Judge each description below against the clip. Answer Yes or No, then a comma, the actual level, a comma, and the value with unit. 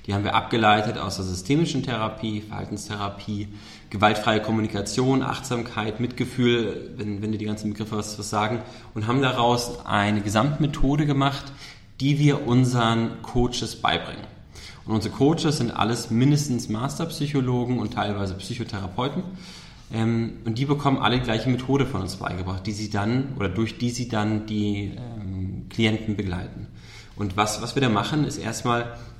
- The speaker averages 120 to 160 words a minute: Yes, average, 150 wpm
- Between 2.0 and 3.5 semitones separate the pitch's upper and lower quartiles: Yes, average, 3.2 semitones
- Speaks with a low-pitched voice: Yes, low, 115 Hz